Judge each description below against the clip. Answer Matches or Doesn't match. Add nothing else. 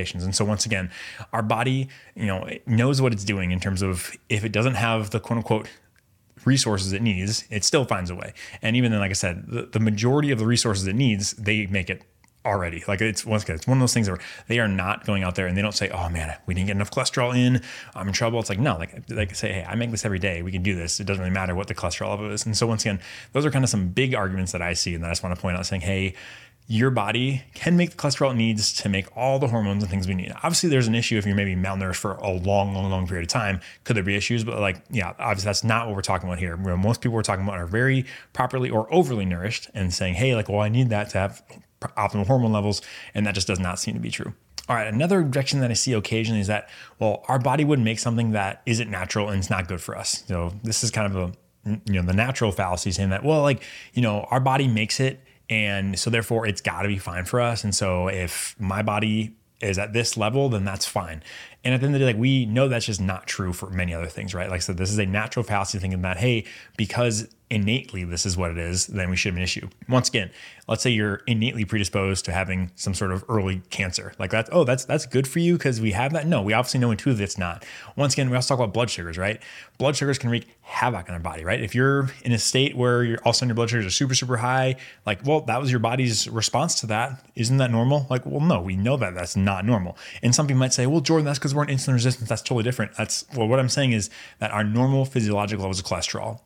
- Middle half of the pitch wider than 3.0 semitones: Matches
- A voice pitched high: Doesn't match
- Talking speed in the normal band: Doesn't match